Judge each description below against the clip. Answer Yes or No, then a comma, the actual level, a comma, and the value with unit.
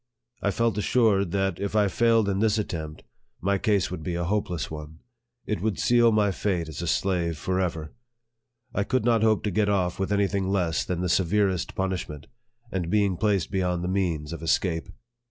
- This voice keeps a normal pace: Yes, average, 190 wpm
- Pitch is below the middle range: Yes, very low, 95 Hz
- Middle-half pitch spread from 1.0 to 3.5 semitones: Yes, average, 3.1 semitones